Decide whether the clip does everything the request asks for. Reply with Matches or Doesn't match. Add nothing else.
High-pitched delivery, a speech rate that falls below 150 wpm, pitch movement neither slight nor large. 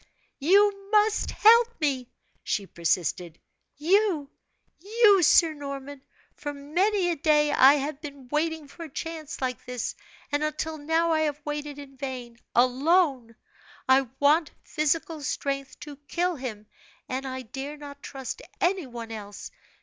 Matches